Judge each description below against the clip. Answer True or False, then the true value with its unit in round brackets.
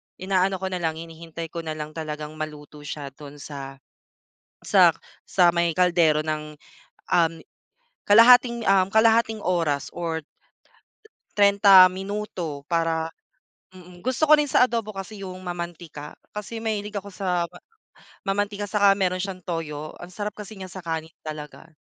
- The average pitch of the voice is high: False (180 Hz)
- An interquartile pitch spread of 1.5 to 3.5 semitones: False (4.0 semitones)